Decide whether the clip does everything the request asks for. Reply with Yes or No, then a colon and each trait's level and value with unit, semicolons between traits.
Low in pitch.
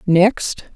No: high, 190 Hz